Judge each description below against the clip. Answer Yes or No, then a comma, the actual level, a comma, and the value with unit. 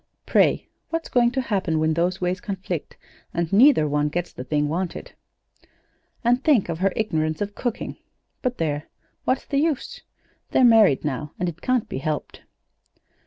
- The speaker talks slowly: No, average, 165 wpm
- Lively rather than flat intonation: Yes, wide, 7.4 semitones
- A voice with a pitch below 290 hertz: Yes, medium, 185 Hz